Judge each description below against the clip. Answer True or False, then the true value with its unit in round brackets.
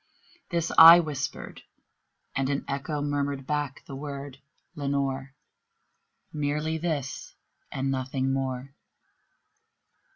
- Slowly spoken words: True (95 wpm)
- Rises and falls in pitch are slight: True (1.8 semitones)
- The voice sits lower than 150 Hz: True (140 Hz)